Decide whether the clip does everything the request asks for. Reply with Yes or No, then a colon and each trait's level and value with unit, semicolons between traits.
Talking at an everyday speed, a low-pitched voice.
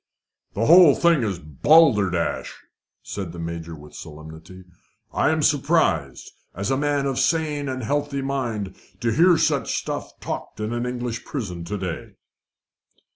Yes: average, 150 wpm; low, 120 Hz